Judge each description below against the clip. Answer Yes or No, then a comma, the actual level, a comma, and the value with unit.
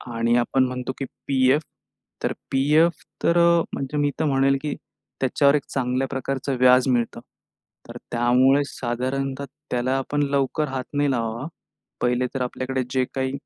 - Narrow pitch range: Yes, narrow, 1.8 semitones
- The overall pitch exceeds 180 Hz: No, low, 135 Hz